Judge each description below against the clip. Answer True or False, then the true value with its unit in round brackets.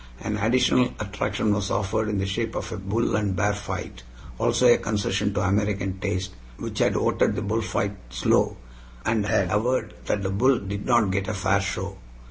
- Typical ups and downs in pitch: False (2.0 semitones)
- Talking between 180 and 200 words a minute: True (185 wpm)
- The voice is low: True (100 Hz)